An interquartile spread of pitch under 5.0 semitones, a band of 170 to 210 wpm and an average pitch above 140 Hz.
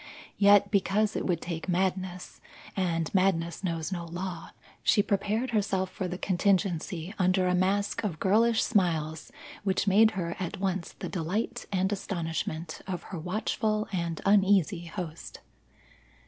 No: average, 2.8 semitones; average, 140 wpm; medium, 185 Hz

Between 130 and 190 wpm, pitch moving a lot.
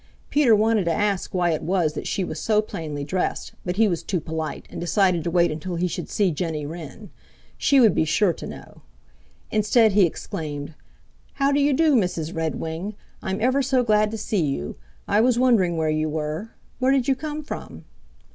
No: average, 200 wpm; wide, 5.7 semitones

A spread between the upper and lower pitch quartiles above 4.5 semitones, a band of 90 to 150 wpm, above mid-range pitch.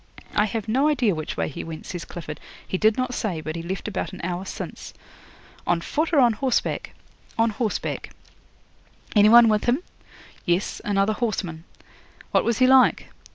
No: average, 5.3 semitones; average, 175 wpm; high, 210 Hz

